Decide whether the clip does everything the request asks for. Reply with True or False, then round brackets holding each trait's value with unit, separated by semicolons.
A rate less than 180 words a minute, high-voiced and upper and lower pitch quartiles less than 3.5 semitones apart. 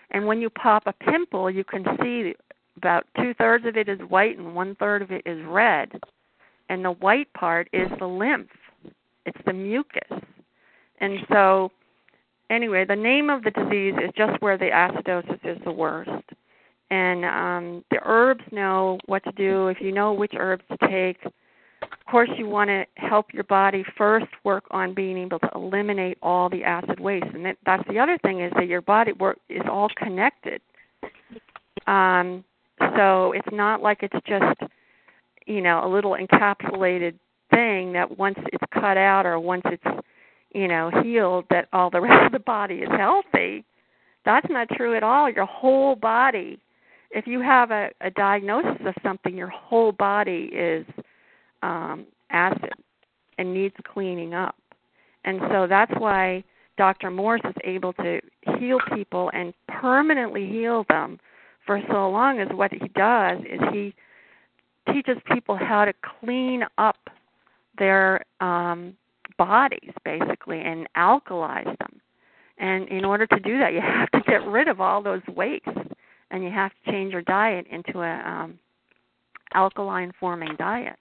True (165 wpm; 195 Hz; 3.1 semitones)